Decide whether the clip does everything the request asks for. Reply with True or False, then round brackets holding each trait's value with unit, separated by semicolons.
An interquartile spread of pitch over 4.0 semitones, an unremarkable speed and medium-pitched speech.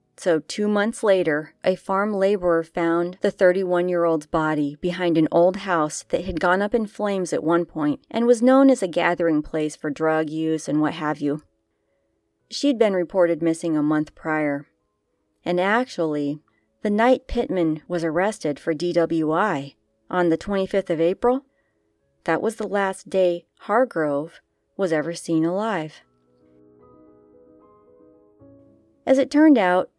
True (4.4 semitones; 150 wpm; 170 Hz)